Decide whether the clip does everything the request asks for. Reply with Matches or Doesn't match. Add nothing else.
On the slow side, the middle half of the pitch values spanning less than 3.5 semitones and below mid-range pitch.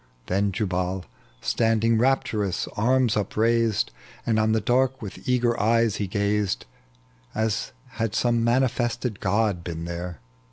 Matches